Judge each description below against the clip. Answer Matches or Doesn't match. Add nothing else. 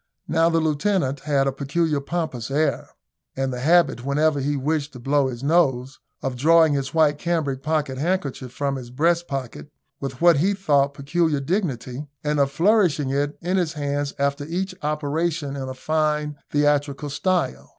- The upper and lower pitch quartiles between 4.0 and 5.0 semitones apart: Doesn't match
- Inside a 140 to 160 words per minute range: Doesn't match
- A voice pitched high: Doesn't match